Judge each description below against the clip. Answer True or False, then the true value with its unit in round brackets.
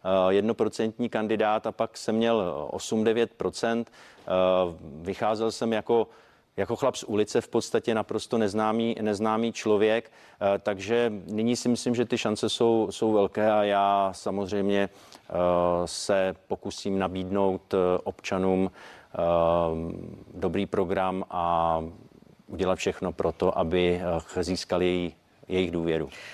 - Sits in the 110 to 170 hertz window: False (100 Hz)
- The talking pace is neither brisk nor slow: False (110 wpm)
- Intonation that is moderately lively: True (3.4 semitones)